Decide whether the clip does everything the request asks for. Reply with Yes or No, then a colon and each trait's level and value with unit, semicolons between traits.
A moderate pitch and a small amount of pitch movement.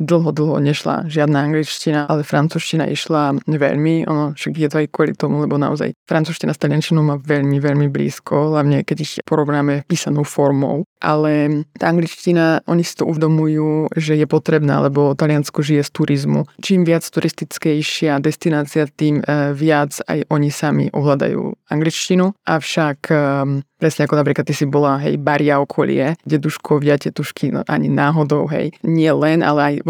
Yes: medium, 150 Hz; narrow, 1.6 semitones